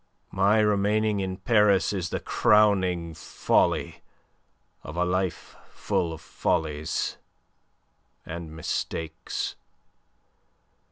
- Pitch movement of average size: Yes, average, 3.8 semitones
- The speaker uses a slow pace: Yes, slow, 90 wpm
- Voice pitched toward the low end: Yes, very low, 95 Hz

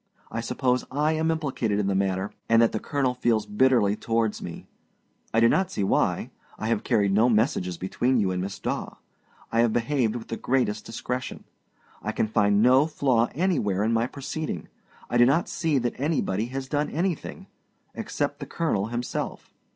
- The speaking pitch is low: Yes, low, 115 Hz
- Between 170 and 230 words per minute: Yes, average, 180 wpm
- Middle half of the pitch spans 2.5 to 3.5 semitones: No, average, 4.3 semitones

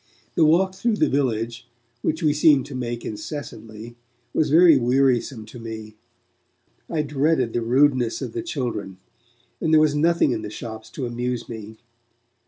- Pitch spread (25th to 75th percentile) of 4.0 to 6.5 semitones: Yes, average, 4.9 semitones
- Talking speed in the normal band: Yes, average, 155 wpm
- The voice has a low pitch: Yes, low, 130 Hz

